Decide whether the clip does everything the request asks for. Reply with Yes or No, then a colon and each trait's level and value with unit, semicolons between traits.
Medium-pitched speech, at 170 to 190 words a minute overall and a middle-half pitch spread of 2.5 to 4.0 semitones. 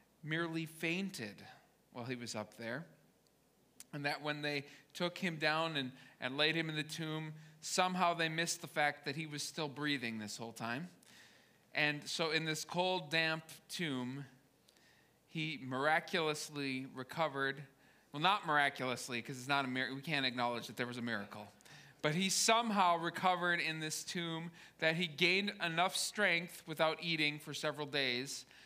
No: medium, 155 Hz; average, 160 wpm; average, 3.5 semitones